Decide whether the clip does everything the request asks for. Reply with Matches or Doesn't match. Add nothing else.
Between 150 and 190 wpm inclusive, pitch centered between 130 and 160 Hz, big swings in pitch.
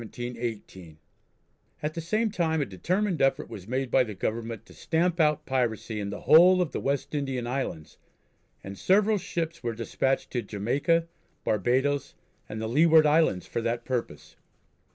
Matches